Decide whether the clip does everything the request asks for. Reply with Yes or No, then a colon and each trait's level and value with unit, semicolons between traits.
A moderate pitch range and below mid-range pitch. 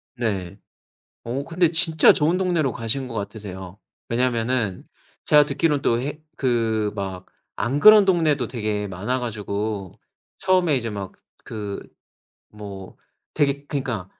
No: wide, 5.9 semitones; low, 120 Hz